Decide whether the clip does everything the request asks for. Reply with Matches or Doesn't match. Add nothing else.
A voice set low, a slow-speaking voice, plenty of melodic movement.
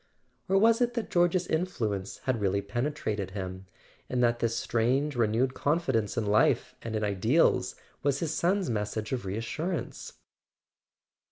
Doesn't match